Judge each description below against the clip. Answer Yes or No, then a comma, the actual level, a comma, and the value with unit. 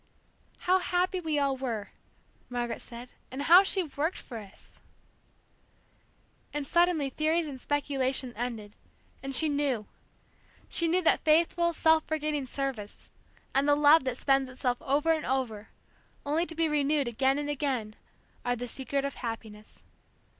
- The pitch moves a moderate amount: Yes, average, 4.0 semitones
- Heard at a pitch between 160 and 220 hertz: No, very high, 280 Hz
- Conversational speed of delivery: Yes, average, 145 wpm